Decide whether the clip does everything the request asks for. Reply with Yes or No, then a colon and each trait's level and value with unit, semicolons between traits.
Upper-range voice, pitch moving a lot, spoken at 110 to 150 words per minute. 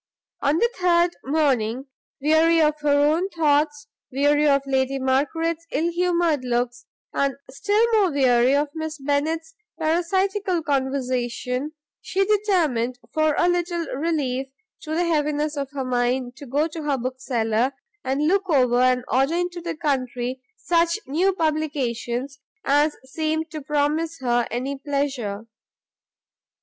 No: very high, 290 Hz; average, 3.9 semitones; slow, 135 wpm